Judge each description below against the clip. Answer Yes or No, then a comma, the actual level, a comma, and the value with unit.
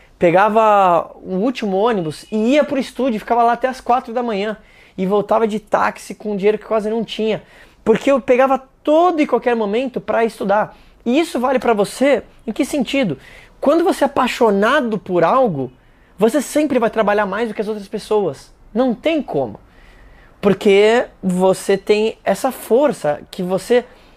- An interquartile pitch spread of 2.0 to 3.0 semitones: No, average, 4.3 semitones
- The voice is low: No, high, 220 Hz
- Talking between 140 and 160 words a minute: No, average, 175 wpm